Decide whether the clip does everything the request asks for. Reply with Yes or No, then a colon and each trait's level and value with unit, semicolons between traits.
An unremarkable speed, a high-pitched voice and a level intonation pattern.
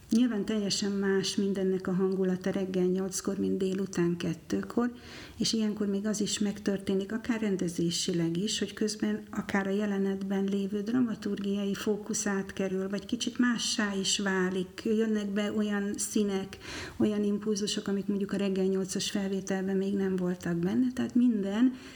Yes: average, 140 wpm; high, 200 Hz; narrow, 1.7 semitones